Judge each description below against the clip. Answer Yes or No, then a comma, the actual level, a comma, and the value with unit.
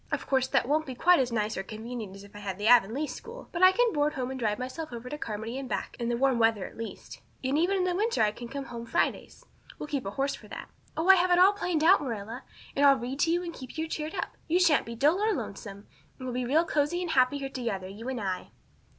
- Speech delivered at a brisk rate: Yes, fast, 275 wpm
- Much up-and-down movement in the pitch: Yes, wide, 5.8 semitones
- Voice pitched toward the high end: Yes, very high, 265 Hz